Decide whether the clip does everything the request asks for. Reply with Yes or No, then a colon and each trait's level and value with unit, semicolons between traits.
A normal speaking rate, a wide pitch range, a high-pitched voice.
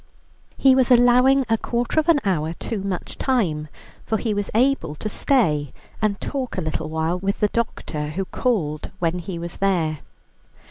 Yes: average, 175 wpm; wide, 7.0 semitones; high, 195 Hz